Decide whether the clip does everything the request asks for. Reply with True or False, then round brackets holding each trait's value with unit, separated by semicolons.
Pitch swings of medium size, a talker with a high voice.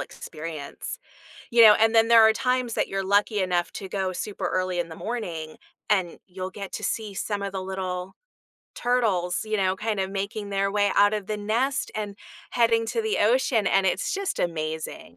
True (3.1 semitones; 200 Hz)